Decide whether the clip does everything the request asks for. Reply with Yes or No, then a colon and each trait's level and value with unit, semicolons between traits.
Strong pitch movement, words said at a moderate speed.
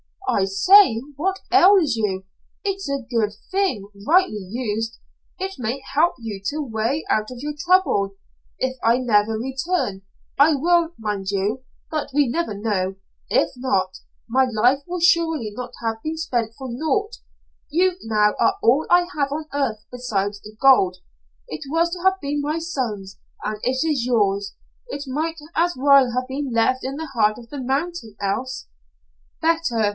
Yes: wide, 6.6 semitones; average, 165 wpm